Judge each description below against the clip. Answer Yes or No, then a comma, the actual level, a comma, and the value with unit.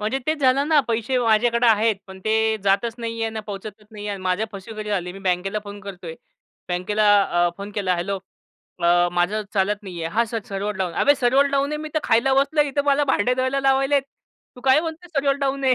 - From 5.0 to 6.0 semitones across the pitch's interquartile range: Yes, wide, 5.4 semitones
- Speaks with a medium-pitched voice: No, high, 220 Hz